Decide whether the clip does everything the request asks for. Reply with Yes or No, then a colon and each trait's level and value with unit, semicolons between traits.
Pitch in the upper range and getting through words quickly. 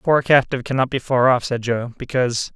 No: low, 125 Hz; fast, 235 wpm